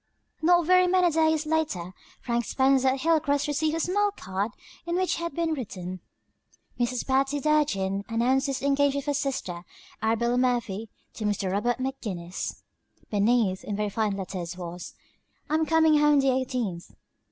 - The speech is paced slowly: No, average, 150 wpm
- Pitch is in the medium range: No, very high, 260 Hz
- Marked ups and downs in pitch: Yes, wide, 6.8 semitones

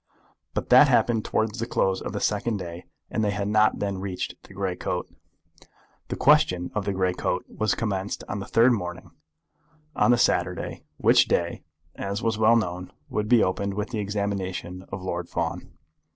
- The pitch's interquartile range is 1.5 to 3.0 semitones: Yes, average, 2.7 semitones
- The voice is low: Yes, low, 100 Hz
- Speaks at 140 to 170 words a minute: No, average, 180 wpm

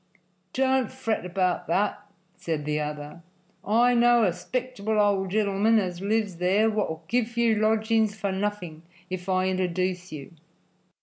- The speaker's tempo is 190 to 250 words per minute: No, average, 140 wpm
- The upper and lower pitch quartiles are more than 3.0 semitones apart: Yes, average, 3.6 semitones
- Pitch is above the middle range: Yes, high, 200 Hz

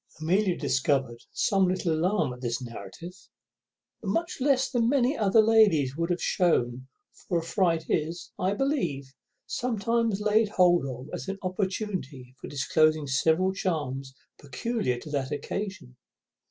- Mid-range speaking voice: Yes, medium, 175 Hz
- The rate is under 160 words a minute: Yes, average, 140 wpm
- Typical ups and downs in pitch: No, wide, 7.1 semitones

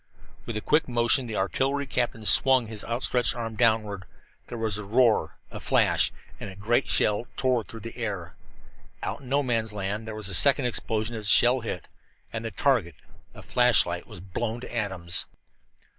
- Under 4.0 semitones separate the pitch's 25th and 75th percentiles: Yes, average, 2.8 semitones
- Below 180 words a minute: No, average, 185 wpm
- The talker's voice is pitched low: Yes, low, 115 Hz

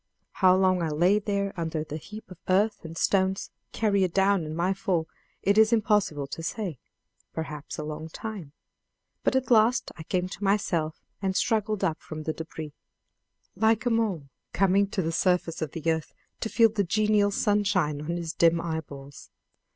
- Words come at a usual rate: Yes, average, 175 wpm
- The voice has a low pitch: No, medium, 185 Hz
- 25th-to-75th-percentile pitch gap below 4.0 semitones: No, average, 4.3 semitones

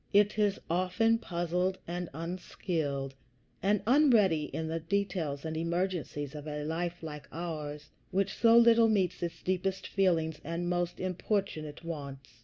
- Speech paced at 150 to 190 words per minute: No, average, 140 wpm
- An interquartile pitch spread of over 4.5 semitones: No, average, 3.5 semitones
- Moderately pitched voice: Yes, medium, 175 Hz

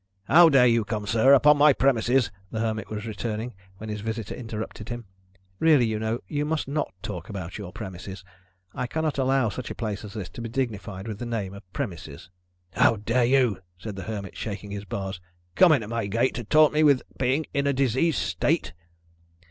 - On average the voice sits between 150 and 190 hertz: No, low, 115 Hz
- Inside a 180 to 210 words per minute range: Yes, fast, 205 wpm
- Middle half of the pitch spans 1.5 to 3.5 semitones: No, average, 4.5 semitones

